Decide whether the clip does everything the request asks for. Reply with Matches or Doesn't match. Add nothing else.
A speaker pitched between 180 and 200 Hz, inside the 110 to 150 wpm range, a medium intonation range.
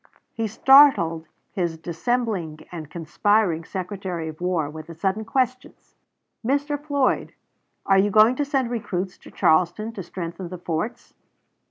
Doesn't match